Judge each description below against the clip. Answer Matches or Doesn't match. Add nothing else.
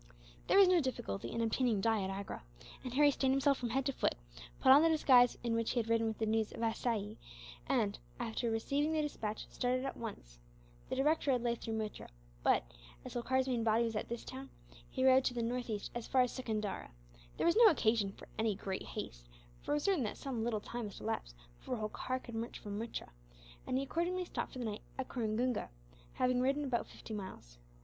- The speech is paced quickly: Matches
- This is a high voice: Matches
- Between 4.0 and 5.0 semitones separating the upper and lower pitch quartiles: Doesn't match